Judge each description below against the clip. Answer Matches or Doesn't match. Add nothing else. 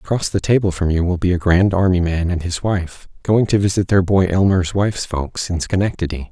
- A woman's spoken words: Doesn't match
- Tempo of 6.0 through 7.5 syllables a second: Doesn't match